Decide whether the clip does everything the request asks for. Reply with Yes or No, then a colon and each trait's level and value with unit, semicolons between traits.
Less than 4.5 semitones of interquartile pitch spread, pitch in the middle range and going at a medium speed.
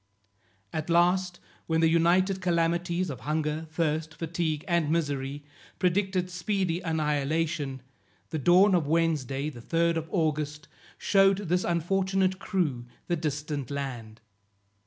No: average, 3.1 semitones; medium, 165 Hz; slow, 120 wpm